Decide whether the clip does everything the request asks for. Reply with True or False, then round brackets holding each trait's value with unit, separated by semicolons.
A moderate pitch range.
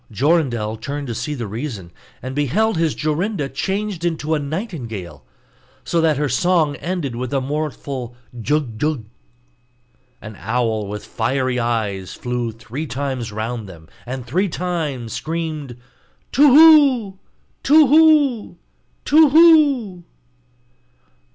False (7.2 semitones)